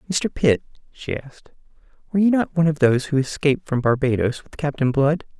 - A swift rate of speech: No, average, 190 wpm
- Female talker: No, male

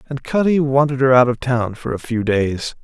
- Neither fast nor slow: No, fast, 235 wpm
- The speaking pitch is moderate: No, low, 130 Hz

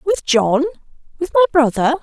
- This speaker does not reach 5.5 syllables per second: Yes, 5.1 syllables/s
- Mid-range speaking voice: No, very high, 300 Hz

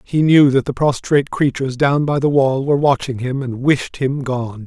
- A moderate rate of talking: No, fast, 220 wpm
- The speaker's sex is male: Yes, male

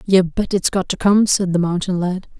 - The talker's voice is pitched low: No, medium, 185 Hz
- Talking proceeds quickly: Yes, fast, 250 wpm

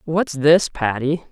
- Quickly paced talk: No, slow, 135 wpm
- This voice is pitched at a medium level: Yes, medium, 145 Hz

